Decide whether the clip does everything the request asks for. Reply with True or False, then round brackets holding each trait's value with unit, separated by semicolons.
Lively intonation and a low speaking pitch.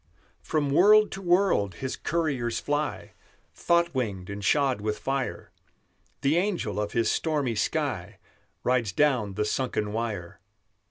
True (6.7 semitones; 130 Hz)